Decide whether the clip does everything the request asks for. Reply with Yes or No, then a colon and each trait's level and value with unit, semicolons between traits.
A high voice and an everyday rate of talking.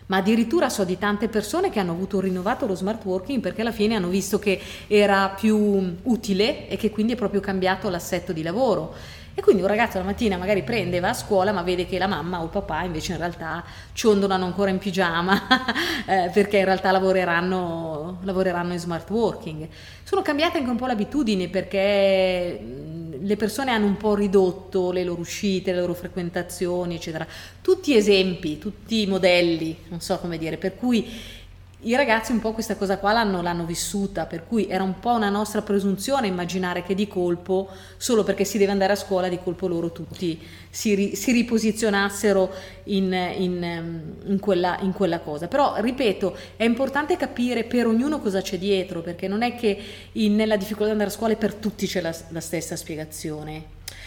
No: high, 195 Hz; fast, 190 wpm